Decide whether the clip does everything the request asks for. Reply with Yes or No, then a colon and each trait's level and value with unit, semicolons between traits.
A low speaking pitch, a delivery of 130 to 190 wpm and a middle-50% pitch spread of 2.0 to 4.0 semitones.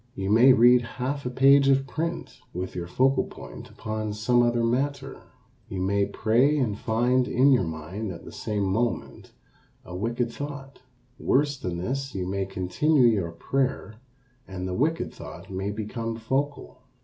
No: low, 120 Hz; average, 160 wpm; wide, 5.4 semitones